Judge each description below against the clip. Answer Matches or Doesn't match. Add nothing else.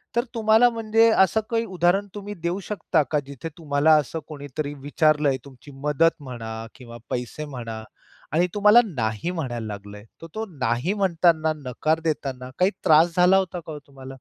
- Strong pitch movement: Matches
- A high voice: Doesn't match